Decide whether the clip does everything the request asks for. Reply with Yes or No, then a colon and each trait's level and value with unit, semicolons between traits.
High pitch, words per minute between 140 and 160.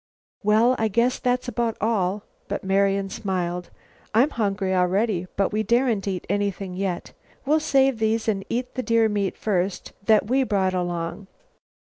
Yes: high, 205 Hz; average, 155 wpm